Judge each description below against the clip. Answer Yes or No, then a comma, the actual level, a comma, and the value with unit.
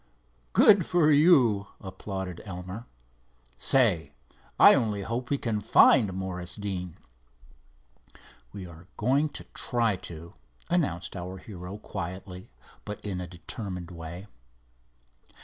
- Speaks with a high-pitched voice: No, very low, 95 Hz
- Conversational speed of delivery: No, slow, 115 wpm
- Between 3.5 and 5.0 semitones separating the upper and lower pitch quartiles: Yes, average, 4.4 semitones